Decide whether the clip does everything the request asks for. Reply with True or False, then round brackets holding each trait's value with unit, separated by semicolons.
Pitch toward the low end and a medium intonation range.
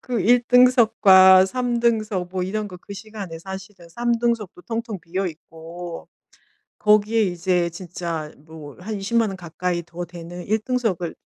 False (190 Hz; 4.2 semitones)